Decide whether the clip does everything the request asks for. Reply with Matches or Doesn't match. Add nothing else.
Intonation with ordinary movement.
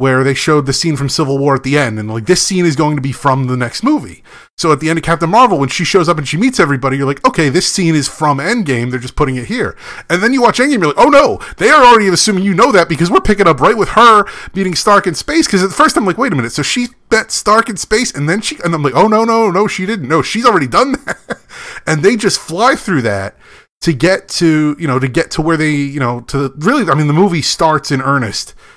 Doesn't match